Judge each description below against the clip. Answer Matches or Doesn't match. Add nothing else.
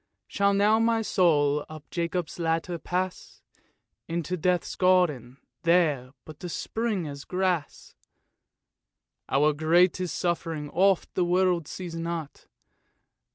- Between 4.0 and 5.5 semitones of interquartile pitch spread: Doesn't match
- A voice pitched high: Doesn't match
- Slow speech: Matches